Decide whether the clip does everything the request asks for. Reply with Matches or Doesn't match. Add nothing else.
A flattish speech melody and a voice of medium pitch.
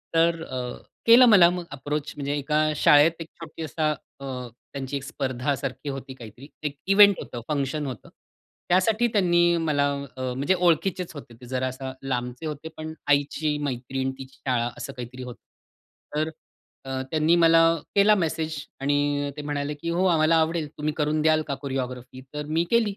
Doesn't match